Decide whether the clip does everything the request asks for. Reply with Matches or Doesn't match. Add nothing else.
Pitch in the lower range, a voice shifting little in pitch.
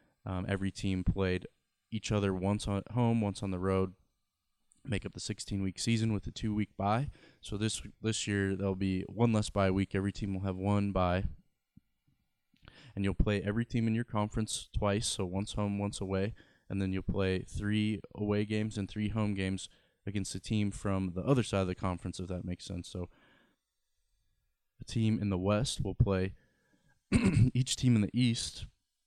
Matches